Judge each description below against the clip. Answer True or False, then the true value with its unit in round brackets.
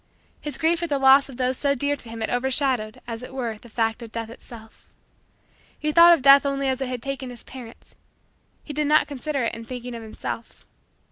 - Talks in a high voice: True (260 Hz)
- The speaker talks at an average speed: False (220 wpm)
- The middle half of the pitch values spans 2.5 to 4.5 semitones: True (3.3 semitones)